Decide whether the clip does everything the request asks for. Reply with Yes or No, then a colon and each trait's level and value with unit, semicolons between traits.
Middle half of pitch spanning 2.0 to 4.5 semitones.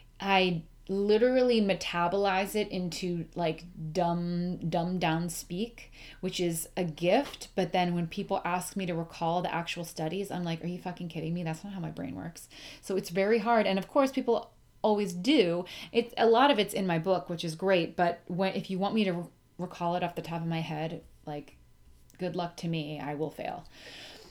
Yes: narrow, 2.5 semitones